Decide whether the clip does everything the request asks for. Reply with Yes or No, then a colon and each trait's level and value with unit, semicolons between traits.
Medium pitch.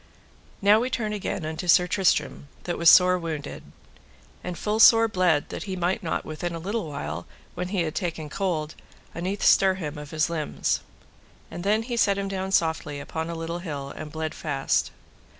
Yes: medium, 175 Hz